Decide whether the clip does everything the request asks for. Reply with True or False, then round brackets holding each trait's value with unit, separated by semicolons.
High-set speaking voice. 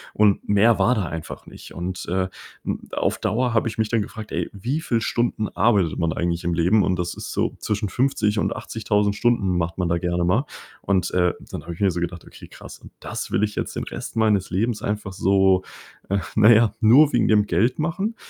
False (105 Hz)